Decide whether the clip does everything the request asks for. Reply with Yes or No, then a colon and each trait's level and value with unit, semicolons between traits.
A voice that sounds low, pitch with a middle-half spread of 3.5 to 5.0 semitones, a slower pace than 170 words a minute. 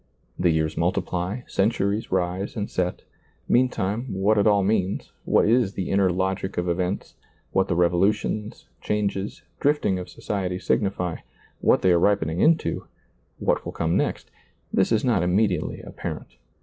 No: very low, 95 Hz; average, 2.8 semitones; average, 150 wpm